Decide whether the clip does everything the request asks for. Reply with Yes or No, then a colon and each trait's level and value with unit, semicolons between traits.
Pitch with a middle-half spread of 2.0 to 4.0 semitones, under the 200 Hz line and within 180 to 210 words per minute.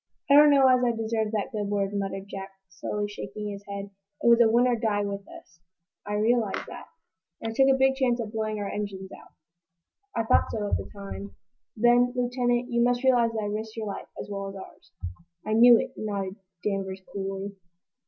No: average, 3.2 semitones; high, 215 Hz; fast, 205 wpm